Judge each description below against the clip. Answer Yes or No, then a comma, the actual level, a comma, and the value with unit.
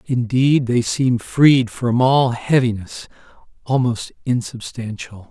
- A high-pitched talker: No, low, 120 Hz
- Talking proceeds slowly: Yes, slow, 100 wpm